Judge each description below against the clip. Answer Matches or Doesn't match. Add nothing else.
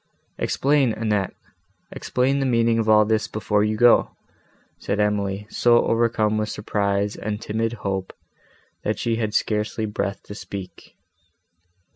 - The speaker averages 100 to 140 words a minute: Matches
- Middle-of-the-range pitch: Doesn't match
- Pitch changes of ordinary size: Doesn't match